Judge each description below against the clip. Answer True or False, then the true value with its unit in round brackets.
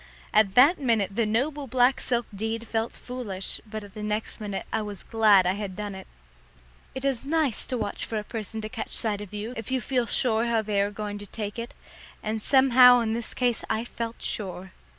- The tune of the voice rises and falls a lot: False (2.8 semitones)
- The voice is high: True (220 Hz)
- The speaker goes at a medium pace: False (215 wpm)